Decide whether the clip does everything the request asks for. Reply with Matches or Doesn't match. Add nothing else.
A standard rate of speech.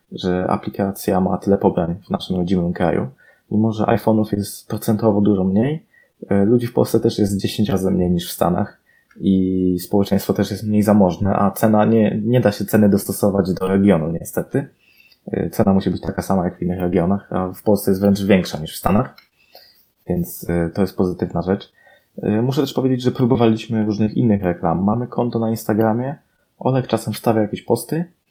Doesn't match